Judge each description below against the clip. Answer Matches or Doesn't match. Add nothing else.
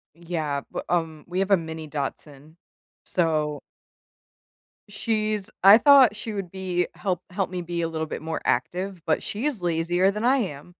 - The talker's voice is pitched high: Doesn't match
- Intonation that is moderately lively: Matches